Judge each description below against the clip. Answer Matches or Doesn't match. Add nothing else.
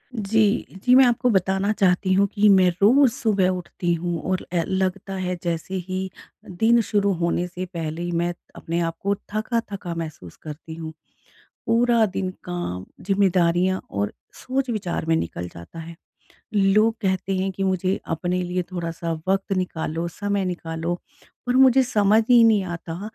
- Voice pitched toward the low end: Doesn't match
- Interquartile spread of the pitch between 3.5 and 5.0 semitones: Doesn't match